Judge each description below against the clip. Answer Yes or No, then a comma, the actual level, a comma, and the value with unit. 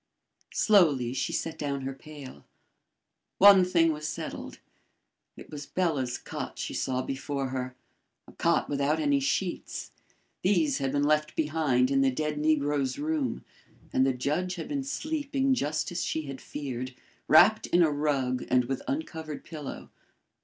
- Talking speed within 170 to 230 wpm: No, average, 155 wpm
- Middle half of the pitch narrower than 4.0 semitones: No, average, 4.3 semitones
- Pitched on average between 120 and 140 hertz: No, medium, 150 Hz